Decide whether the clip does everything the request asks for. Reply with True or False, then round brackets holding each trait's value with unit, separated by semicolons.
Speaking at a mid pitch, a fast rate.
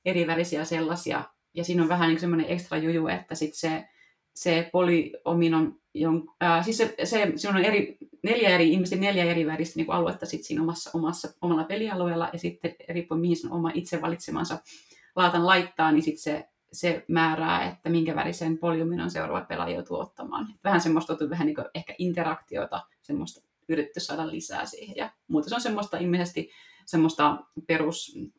True (165 Hz; 175 wpm)